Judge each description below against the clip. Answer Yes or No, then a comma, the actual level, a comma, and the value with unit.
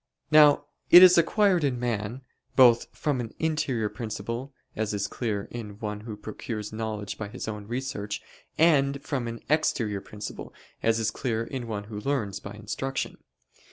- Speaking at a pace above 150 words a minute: Yes, average, 160 wpm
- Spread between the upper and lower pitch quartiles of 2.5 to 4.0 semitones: No, average, 4.4 semitones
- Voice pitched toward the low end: Yes, low, 115 Hz